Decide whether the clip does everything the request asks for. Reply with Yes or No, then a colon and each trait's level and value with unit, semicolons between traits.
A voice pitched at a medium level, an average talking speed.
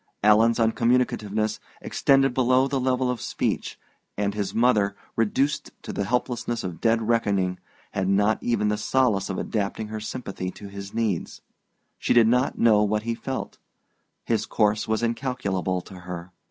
No: low, 110 Hz; average, 155 wpm